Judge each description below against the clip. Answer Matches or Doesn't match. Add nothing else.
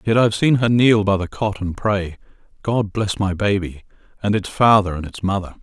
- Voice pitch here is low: Matches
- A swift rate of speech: Matches